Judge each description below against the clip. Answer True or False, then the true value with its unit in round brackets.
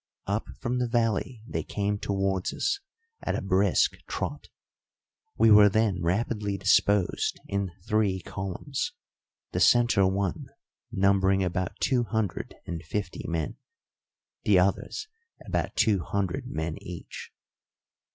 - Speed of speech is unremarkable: False (120 wpm)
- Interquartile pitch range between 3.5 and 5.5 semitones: False (2.7 semitones)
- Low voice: True (100 Hz)